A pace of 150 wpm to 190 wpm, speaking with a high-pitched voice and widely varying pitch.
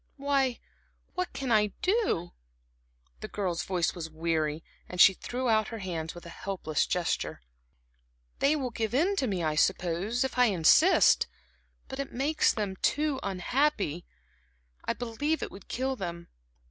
Yes: average, 155 wpm; high, 215 Hz; wide, 7.4 semitones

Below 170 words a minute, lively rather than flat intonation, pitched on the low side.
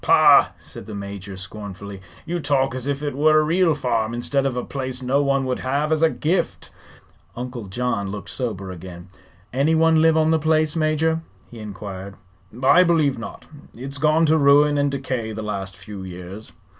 No: average, 180 wpm; wide, 6.8 semitones; low, 130 Hz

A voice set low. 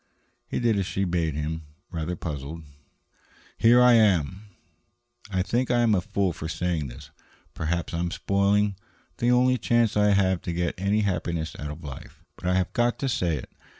Yes: very low, 95 Hz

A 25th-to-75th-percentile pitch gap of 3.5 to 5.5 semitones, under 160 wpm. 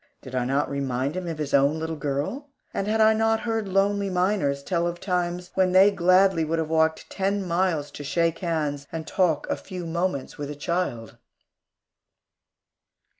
No: average, 4.4 semitones; average, 175 wpm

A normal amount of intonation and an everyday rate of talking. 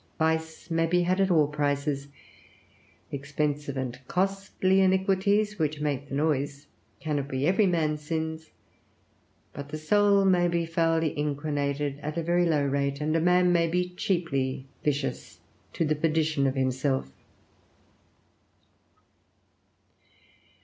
No: average, 3.6 semitones; slow, 130 wpm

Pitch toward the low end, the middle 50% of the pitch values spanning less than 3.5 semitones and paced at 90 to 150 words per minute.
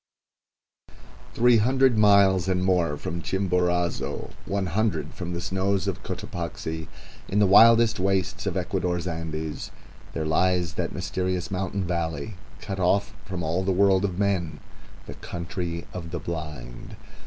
Yes: very low, 90 Hz; narrow, 2.6 semitones; slow, 135 wpm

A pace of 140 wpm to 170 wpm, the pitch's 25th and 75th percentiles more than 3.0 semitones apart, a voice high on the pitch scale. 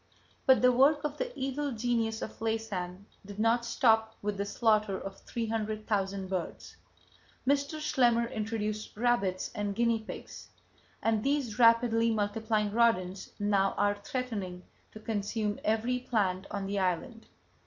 No: average, 145 wpm; average, 2.7 semitones; high, 220 Hz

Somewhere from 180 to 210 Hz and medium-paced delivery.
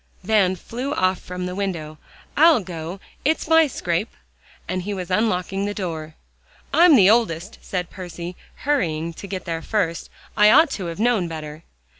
Yes: medium, 185 Hz; average, 165 wpm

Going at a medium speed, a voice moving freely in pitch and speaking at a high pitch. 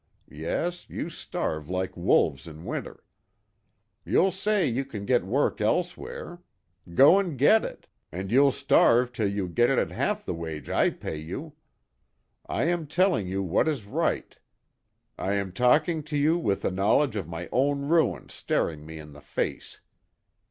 No: average, 165 wpm; wide, 8.9 semitones; low, 120 Hz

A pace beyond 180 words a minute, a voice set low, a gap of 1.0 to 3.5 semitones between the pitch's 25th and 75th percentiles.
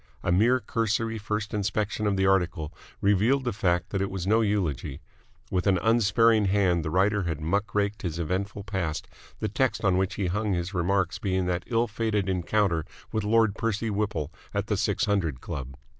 Yes: average, 190 wpm; low, 100 Hz; average, 3.1 semitones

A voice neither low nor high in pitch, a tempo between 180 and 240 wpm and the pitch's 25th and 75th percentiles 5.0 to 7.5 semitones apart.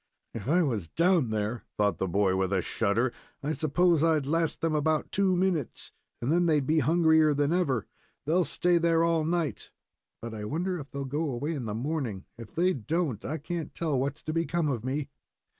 Yes: medium, 150 Hz; average, 200 wpm; wide, 5.5 semitones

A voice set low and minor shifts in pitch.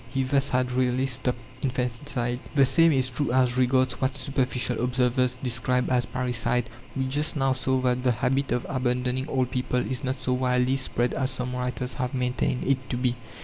Yes: low, 125 Hz; narrow, 0.9 semitones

